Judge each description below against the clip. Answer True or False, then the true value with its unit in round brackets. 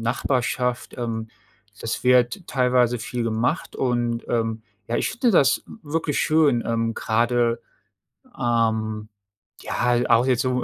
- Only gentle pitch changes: True (1.8 semitones)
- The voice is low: True (120 Hz)